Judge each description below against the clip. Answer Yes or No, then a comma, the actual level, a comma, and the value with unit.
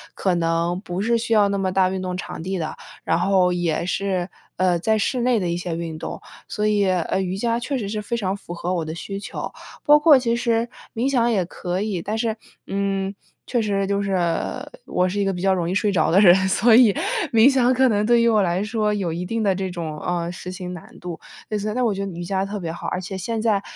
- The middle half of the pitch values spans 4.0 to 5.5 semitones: No, average, 3.6 semitones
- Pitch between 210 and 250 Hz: No, high, 195 Hz